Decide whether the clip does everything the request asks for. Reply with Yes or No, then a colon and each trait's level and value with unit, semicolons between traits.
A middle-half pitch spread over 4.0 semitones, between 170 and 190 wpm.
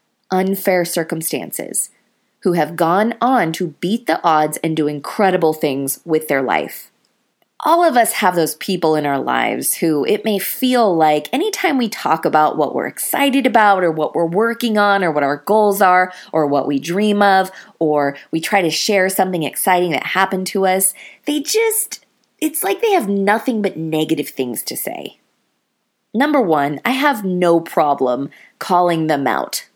Yes: wide, 5.5 semitones; average, 175 wpm